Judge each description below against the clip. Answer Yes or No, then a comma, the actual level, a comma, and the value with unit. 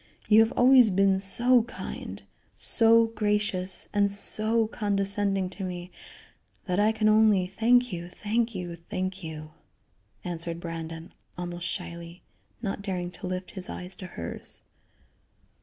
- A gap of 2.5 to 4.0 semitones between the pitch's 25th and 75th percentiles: Yes, average, 3.2 semitones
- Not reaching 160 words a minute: Yes, slow, 135 wpm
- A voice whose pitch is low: No, high, 195 Hz